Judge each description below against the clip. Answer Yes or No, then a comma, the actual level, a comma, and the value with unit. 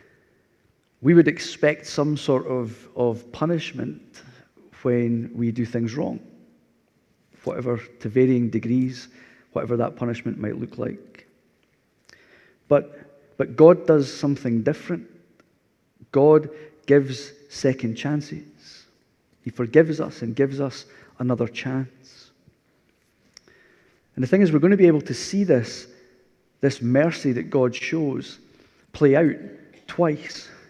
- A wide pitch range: No, average, 3.7 semitones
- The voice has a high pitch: No, low, 135 Hz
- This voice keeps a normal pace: No, slow, 115 wpm